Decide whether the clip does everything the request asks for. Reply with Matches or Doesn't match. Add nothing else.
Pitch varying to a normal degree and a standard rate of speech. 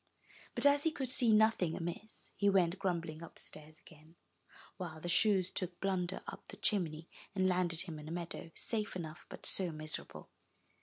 Matches